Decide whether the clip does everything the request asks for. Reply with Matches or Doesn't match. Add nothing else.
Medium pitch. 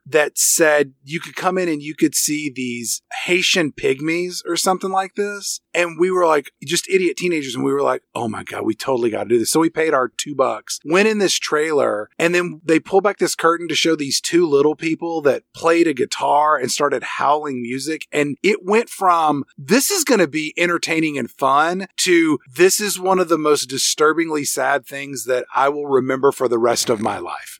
Matches